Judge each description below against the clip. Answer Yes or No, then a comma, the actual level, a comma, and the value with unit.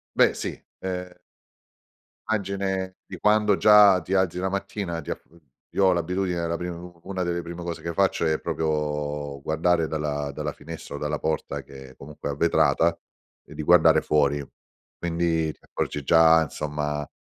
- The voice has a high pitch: No, very low, 85 Hz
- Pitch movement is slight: No, average, 3.4 semitones